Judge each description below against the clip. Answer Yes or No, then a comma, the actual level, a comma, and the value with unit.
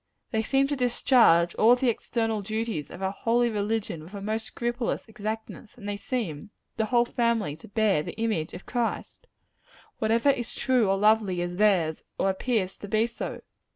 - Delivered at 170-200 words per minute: Yes, average, 180 wpm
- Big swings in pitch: No, average, 3.4 semitones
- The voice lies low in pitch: No, high, 220 Hz